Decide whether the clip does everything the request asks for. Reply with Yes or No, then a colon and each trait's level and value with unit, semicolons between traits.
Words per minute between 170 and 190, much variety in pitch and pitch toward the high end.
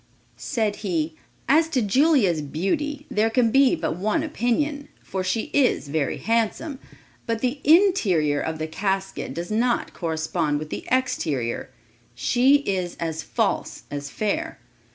No: average, 140 wpm; wide, 9.0 semitones; high, 215 Hz